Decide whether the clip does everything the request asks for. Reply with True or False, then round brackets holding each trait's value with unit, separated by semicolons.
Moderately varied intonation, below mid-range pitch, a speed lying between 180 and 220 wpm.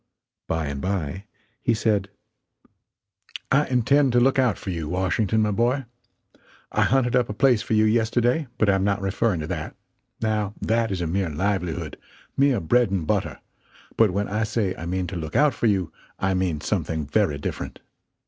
True (4.5 semitones; 100 Hz; 185 wpm)